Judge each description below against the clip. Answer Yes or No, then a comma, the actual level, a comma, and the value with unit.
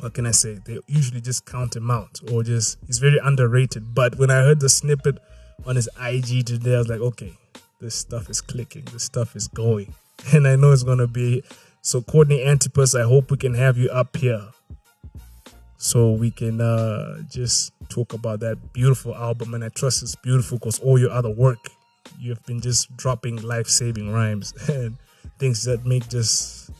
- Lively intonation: No, narrow, 2.4 semitones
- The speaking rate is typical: Yes, average, 190 wpm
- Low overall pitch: Yes, low, 120 Hz